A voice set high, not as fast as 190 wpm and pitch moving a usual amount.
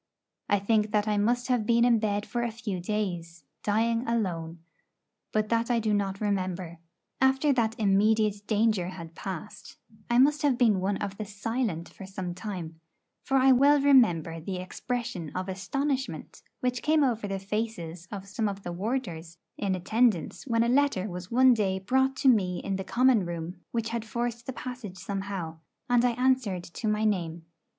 Yes: high, 210 Hz; average, 180 wpm; average, 4.2 semitones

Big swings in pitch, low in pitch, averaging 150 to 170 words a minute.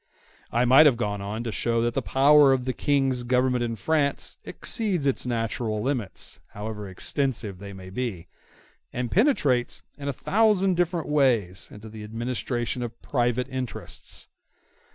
No: average, 4.0 semitones; low, 125 Hz; average, 155 wpm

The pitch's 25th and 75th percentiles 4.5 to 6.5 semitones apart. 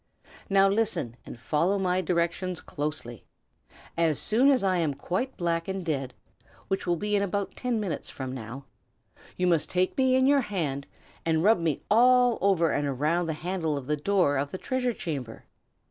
Yes: average, 5.1 semitones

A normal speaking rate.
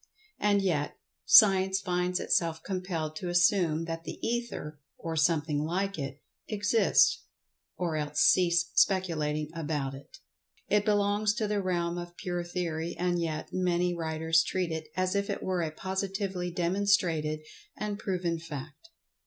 Yes: average, 145 wpm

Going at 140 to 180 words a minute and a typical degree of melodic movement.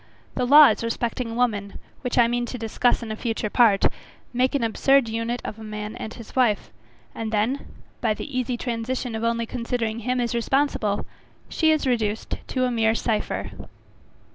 No: average, 175 wpm; narrow, 2.2 semitones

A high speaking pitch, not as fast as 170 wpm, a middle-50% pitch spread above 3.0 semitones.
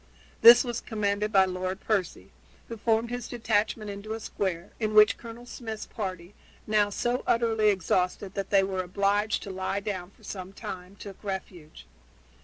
No: high, 205 Hz; average, 160 wpm; narrow, 2.6 semitones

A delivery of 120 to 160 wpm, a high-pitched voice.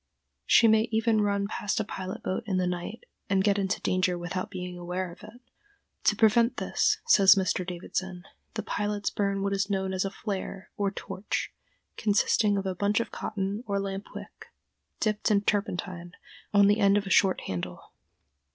No: average, 180 wpm; high, 200 Hz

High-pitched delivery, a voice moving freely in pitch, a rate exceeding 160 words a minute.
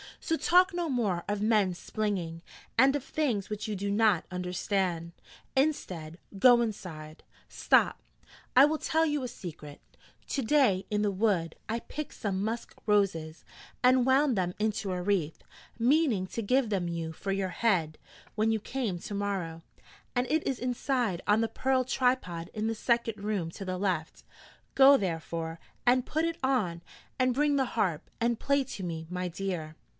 Yes: high, 210 Hz; wide, 6.0 semitones; average, 170 wpm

